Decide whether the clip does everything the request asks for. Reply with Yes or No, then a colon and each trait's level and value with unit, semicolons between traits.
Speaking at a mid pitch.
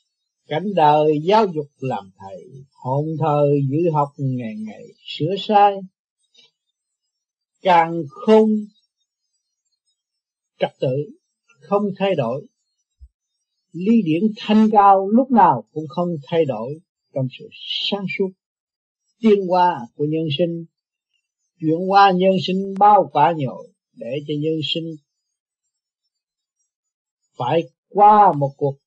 Yes: medium, 175 Hz